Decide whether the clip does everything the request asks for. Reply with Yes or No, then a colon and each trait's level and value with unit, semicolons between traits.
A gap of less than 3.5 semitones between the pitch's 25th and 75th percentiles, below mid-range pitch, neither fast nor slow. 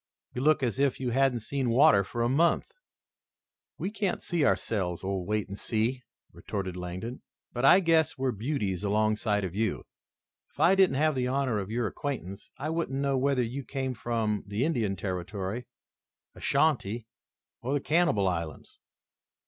No: wide, 5.5 semitones; low, 120 Hz; average, 165 wpm